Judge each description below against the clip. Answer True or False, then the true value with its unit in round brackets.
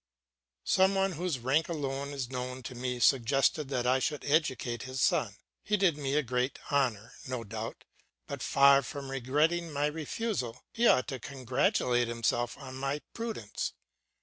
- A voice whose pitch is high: False (135 Hz)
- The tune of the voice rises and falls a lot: False (3.2 semitones)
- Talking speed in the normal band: True (160 wpm)